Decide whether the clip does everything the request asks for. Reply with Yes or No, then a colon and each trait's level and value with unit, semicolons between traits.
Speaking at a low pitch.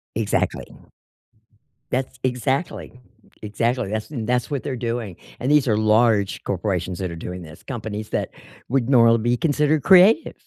Yes: low, 115 Hz